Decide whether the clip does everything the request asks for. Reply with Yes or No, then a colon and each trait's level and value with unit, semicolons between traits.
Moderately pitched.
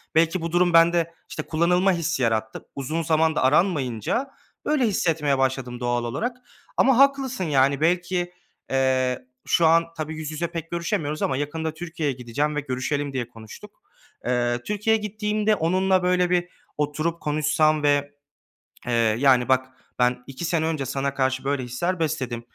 Yes: medium, 155 Hz